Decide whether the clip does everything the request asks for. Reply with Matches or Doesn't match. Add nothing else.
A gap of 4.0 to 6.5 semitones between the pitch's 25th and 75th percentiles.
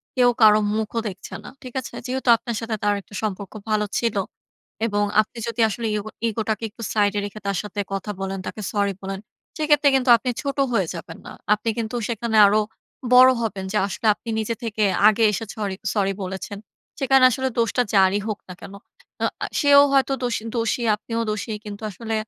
Doesn't match